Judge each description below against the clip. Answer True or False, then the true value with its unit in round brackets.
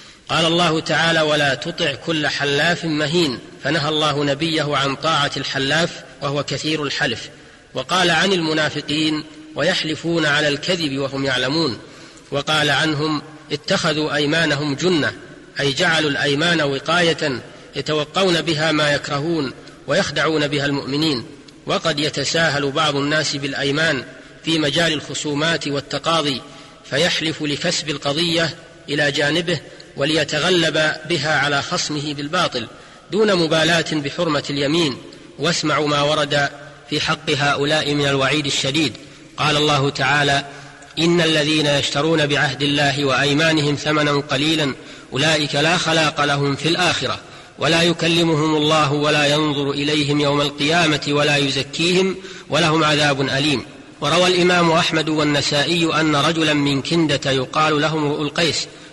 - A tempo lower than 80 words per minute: False (115 wpm)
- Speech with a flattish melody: True (2.2 semitones)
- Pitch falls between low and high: True (150 Hz)